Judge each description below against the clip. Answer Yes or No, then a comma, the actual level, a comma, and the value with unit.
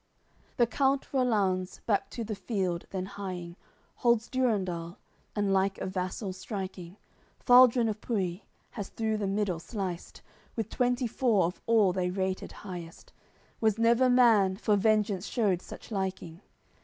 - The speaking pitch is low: No, high, 200 Hz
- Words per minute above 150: No, average, 145 wpm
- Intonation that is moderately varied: Yes, average, 3.6 semitones